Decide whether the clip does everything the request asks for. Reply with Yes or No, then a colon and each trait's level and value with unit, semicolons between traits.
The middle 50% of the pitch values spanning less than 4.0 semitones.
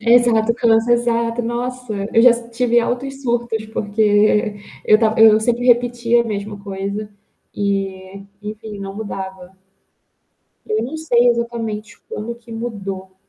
Yes: narrow, 2.5 semitones